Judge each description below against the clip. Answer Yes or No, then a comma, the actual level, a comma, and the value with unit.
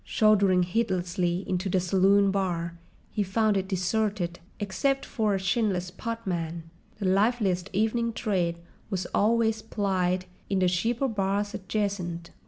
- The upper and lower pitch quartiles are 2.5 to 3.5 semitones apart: Yes, average, 3.0 semitones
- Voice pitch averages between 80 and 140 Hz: No, high, 195 Hz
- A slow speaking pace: Yes, slow, 130 wpm